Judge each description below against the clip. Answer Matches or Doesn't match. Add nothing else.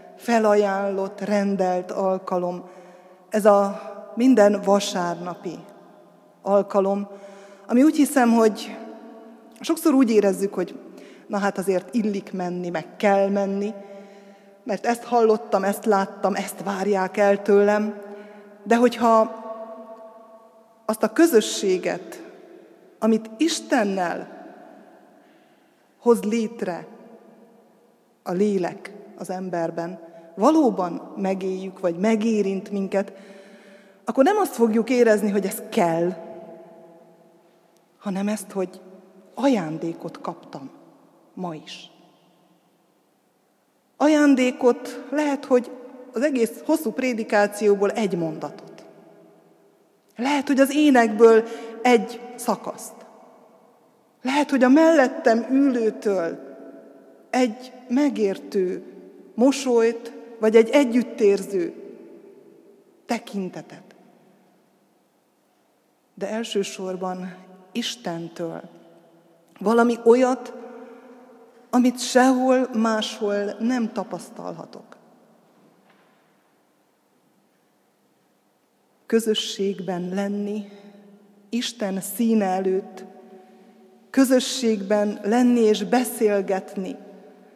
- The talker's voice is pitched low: Doesn't match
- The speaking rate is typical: Doesn't match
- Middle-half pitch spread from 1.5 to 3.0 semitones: Doesn't match